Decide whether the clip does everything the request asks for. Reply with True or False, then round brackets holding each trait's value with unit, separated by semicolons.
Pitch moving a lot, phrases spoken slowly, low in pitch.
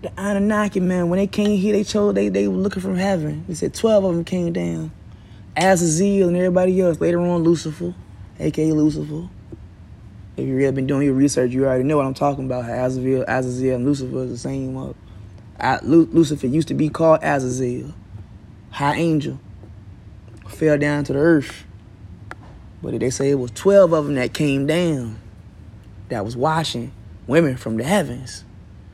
False (8.3 semitones; 170 wpm; 130 Hz)